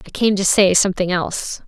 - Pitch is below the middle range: No, high, 190 Hz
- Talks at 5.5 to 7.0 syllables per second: Yes, 6.0 syllables/s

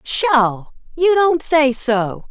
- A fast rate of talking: No, slow, 130 wpm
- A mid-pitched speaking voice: No, very high, 275 Hz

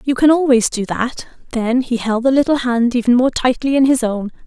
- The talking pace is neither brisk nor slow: No, fast, 230 wpm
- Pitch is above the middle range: Yes, very high, 250 Hz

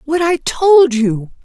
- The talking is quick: No, average, 165 wpm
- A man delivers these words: No, female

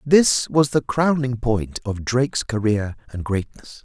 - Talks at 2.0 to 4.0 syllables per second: Yes, 3.9 syllables/s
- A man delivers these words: Yes, male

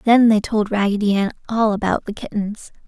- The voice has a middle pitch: No, high, 210 Hz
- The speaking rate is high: No, average, 190 wpm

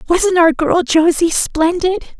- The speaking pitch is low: No, very high, 335 Hz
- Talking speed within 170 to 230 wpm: No, slow, 135 wpm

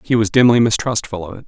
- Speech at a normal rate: No, fast, 245 wpm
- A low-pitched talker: Yes, low, 110 Hz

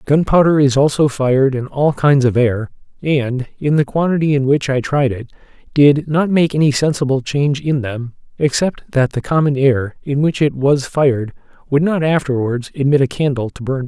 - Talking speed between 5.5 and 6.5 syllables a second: No, 5.1 syllables/s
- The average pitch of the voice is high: No, medium, 140 Hz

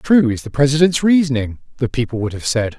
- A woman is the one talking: No, male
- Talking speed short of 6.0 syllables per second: No, 6.5 syllables/s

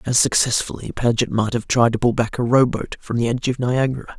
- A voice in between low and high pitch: No, low, 120 Hz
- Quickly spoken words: Yes, fast, 245 wpm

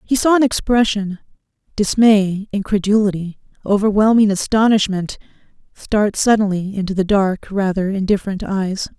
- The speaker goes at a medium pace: No, slow, 95 wpm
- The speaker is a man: No, female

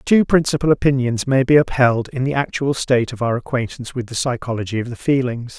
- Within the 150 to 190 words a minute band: No, fast, 205 wpm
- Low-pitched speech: Yes, low, 130 Hz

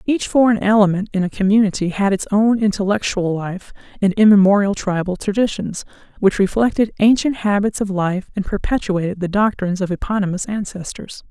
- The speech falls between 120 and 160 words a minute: Yes, average, 150 wpm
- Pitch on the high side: Yes, high, 200 Hz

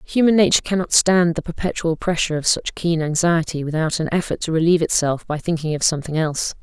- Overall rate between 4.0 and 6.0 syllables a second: No, 6.4 syllables/s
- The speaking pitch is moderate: Yes, medium, 165 Hz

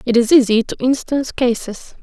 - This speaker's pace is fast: No, average, 180 wpm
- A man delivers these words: No, female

